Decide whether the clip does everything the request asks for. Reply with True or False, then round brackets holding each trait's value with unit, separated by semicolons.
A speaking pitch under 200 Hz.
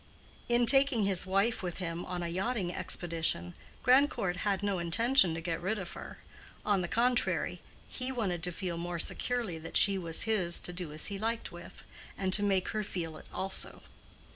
True (190 Hz)